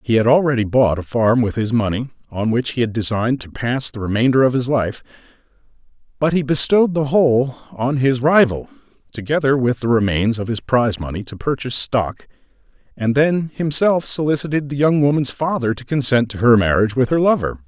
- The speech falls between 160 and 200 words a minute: Yes, average, 190 wpm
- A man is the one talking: Yes, male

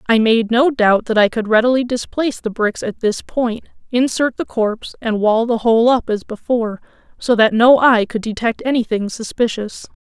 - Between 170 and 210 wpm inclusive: Yes, average, 190 wpm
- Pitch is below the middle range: No, high, 230 Hz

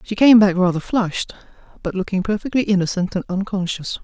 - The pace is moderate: Yes, average, 165 wpm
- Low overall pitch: No, high, 195 Hz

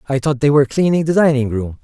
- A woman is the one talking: No, male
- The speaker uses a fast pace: Yes, fast, 260 wpm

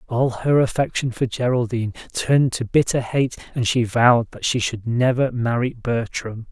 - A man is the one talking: Yes, male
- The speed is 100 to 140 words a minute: No, average, 165 wpm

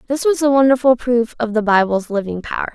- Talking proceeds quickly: Yes, fast, 220 wpm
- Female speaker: Yes, female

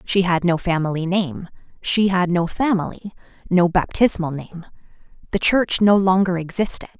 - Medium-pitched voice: Yes, medium, 180 Hz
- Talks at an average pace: Yes, average, 145 wpm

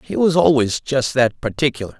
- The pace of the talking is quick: No, average, 180 wpm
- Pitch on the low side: Yes, low, 130 Hz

